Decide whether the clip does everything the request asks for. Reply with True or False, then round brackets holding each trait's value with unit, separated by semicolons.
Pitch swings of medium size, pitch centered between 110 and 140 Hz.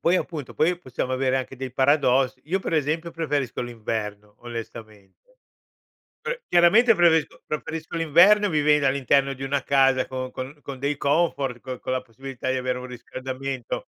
True (3.6 semitones; 135 Hz)